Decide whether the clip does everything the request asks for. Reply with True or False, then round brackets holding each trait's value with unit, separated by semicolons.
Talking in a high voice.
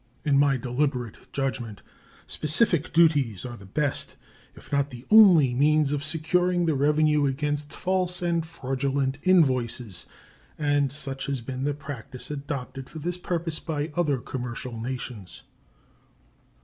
False (145 Hz)